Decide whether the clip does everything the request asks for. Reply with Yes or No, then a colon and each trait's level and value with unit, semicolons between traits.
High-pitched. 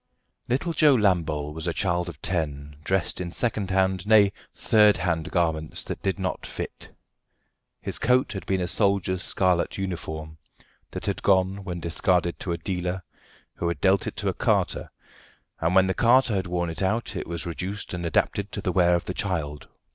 No: very low, 90 Hz